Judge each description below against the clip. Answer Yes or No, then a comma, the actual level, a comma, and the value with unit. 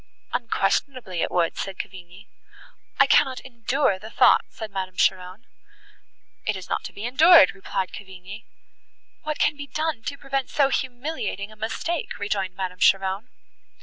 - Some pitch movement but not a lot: No, wide, 5.9 semitones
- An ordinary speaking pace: Yes, average, 150 wpm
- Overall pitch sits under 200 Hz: No, high, 215 Hz